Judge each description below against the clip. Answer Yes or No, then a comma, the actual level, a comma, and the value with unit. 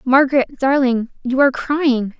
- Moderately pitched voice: No, very high, 260 Hz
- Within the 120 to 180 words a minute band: Yes, slow, 135 wpm